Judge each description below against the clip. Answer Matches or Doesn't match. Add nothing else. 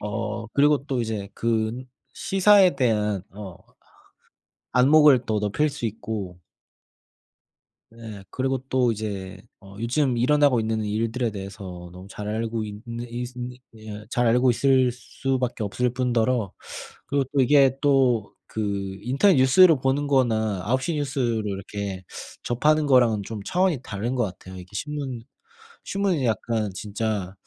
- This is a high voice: Doesn't match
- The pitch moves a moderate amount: Matches